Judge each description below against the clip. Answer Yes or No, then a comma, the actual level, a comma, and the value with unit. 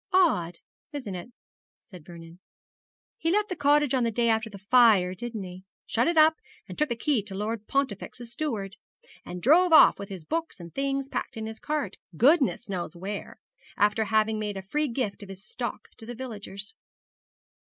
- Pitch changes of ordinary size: No, wide, 5.9 semitones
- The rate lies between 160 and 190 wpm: Yes, average, 185 wpm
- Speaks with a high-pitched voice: Yes, high, 225 Hz